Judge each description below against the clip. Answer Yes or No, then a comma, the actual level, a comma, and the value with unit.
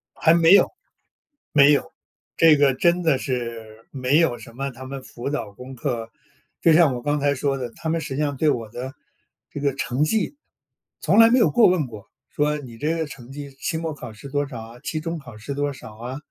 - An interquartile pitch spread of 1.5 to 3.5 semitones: No, average, 4.0 semitones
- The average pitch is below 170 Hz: Yes, medium, 140 Hz